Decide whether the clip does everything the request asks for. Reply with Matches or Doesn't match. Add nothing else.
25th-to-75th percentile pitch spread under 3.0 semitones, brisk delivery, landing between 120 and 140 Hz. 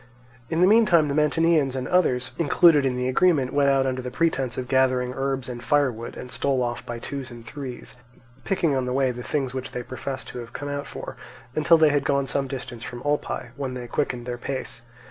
Matches